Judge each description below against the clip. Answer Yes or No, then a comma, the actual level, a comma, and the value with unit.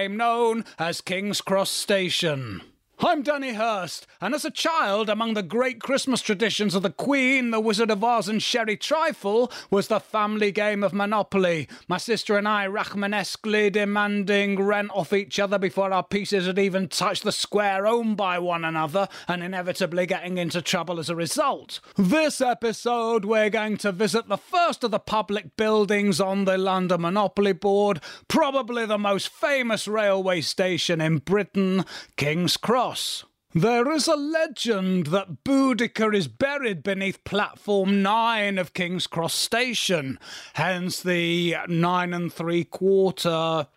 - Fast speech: No, average, 150 wpm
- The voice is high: Yes, high, 200 Hz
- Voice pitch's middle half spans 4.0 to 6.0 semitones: No, average, 3.5 semitones